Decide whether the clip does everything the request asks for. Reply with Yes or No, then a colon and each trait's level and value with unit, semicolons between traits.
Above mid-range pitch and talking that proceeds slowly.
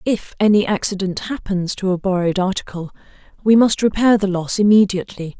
No: high, 195 Hz; average, 155 wpm